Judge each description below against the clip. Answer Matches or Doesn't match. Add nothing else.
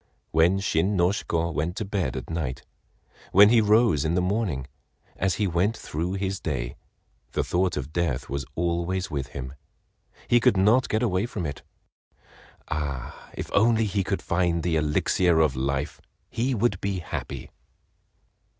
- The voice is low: Matches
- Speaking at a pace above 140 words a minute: Matches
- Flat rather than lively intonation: Doesn't match